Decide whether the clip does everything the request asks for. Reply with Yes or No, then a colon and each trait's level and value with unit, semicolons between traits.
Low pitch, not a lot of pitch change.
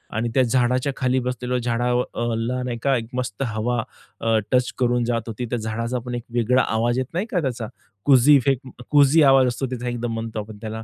Yes: low, 125 Hz; narrow, 1.7 semitones